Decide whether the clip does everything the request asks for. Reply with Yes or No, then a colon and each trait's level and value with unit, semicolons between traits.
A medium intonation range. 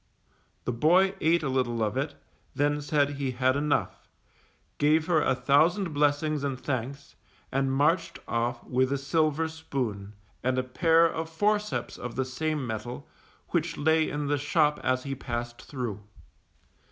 Yes: average, 3.6 semitones